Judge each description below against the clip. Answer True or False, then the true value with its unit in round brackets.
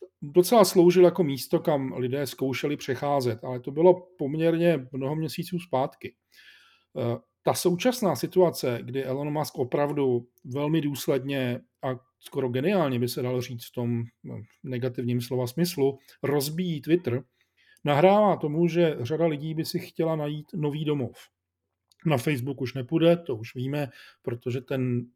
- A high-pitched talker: False (140 Hz)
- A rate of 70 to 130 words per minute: False (140 wpm)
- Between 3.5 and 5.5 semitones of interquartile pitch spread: True (4.8 semitones)